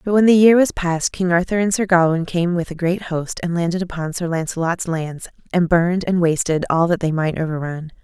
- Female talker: Yes, female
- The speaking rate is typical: No, fast, 230 wpm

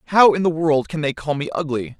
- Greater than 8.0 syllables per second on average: No, 5.9 syllables/s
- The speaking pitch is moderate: Yes, medium, 155 Hz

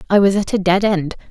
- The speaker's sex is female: Yes, female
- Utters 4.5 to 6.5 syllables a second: Yes, 6.0 syllables/s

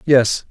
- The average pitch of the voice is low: Yes, low, 130 Hz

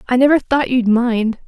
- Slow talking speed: No, fast, 205 wpm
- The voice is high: Yes, high, 245 Hz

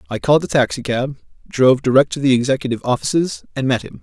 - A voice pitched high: No, low, 135 Hz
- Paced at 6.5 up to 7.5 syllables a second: Yes, 7.0 syllables/s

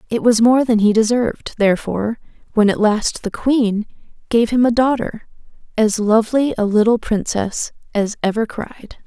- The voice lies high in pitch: Yes, high, 220 Hz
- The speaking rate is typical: Yes, average, 150 wpm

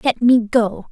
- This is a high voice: Yes, high, 230 Hz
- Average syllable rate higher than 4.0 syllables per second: No, 3.9 syllables/s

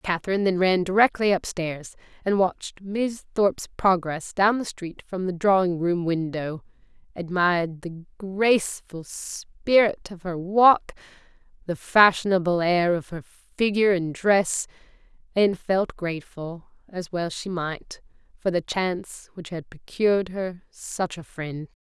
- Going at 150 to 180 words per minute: No, slow, 135 wpm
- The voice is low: No, medium, 185 Hz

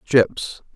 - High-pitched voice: No, low, 110 Hz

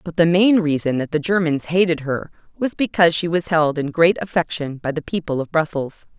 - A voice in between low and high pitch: Yes, medium, 165 Hz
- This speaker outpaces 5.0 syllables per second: Yes, 5.4 syllables/s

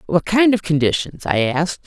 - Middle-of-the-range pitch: Yes, medium, 175 Hz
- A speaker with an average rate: Yes, average, 195 wpm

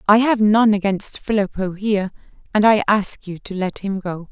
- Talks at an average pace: Yes, average, 195 wpm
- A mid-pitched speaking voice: No, high, 200 Hz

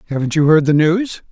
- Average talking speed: No, fast, 225 wpm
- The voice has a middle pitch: Yes, medium, 160 Hz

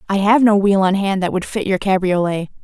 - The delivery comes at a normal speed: No, fast, 250 wpm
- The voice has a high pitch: Yes, high, 195 Hz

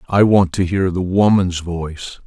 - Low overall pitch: Yes, very low, 90 Hz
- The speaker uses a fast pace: No, average, 185 wpm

